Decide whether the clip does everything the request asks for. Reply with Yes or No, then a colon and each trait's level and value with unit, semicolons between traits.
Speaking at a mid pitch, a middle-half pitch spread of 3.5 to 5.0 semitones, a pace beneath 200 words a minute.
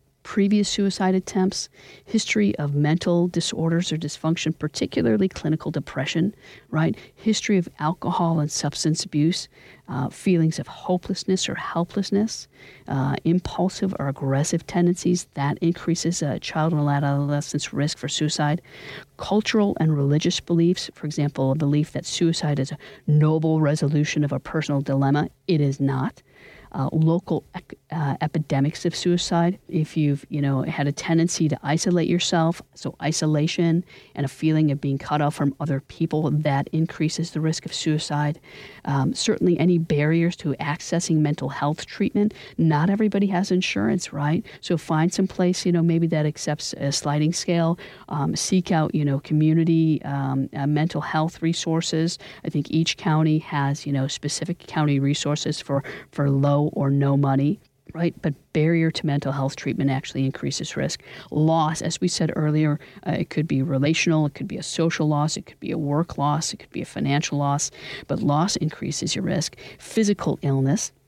No: medium, 155 Hz; average, 2.9 semitones; average, 165 wpm